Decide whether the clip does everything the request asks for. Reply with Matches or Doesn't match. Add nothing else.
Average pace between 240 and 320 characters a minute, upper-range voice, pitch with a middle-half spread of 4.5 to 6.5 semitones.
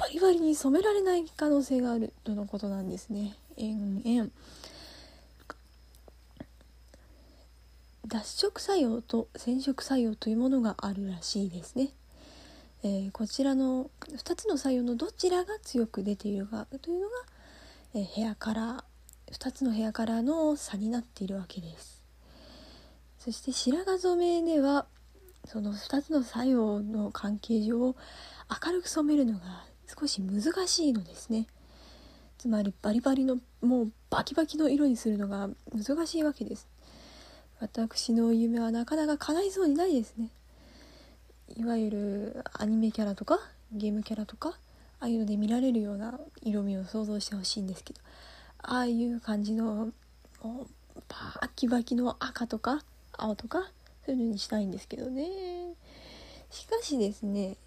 Matches